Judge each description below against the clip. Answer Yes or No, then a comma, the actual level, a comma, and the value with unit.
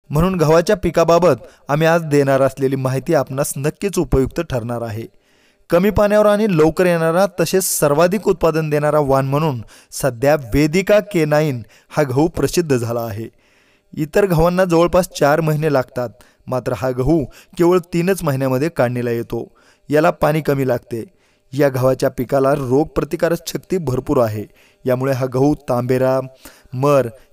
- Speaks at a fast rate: Yes, fast, 135 wpm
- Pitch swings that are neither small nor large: Yes, average, 4.5 semitones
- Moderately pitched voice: Yes, medium, 145 Hz